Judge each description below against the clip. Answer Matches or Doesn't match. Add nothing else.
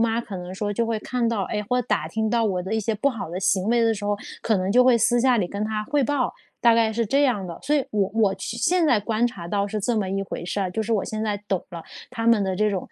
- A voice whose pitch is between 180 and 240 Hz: Matches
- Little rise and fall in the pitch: Doesn't match